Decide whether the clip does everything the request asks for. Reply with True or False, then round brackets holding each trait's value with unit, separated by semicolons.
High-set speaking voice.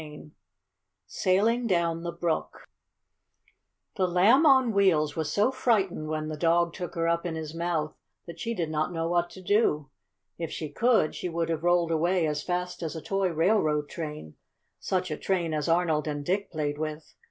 False (170 Hz)